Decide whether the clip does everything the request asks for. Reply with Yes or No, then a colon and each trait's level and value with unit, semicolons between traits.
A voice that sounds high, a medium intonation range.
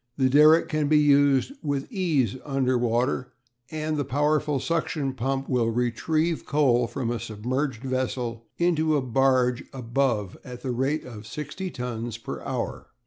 No: low, 135 Hz; average, 3.5 semitones